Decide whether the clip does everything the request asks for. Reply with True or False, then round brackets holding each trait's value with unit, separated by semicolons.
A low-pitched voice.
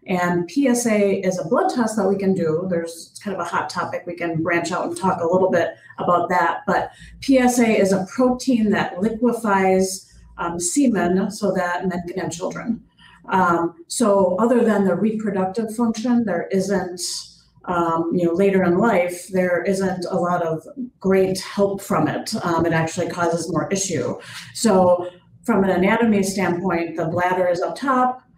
False (185 Hz)